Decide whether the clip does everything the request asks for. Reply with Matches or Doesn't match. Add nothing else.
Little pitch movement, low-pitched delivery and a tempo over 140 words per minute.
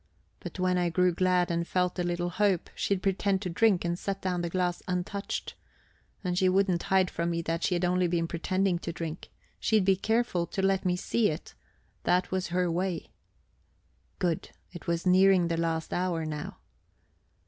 Doesn't match